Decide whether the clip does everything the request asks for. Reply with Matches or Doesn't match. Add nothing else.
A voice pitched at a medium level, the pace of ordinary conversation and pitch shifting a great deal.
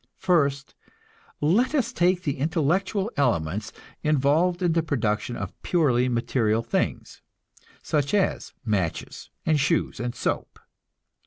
Doesn't match